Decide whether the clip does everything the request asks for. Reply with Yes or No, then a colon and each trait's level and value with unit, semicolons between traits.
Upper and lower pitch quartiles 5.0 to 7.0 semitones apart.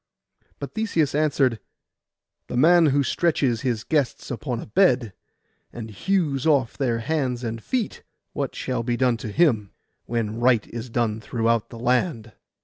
No: average, 4.1 semitones